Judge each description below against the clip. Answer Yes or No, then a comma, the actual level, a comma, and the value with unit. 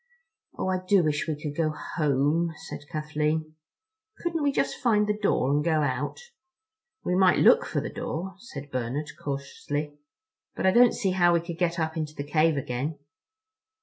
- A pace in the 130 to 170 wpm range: No, average, 180 wpm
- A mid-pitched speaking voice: Yes, medium, 155 Hz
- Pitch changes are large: No, average, 3.9 semitones